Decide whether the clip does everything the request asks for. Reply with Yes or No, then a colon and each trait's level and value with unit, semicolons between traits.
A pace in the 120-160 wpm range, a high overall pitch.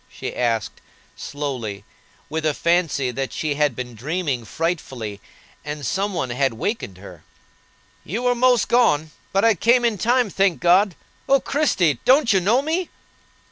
No: average, 155 wpm; medium, 165 Hz